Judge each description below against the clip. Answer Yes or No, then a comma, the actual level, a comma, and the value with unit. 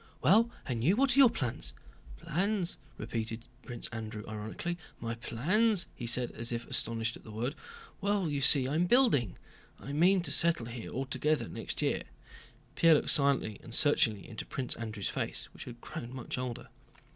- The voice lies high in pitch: No, low, 130 Hz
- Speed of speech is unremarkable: Yes, average, 170 wpm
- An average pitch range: No, wide, 6.7 semitones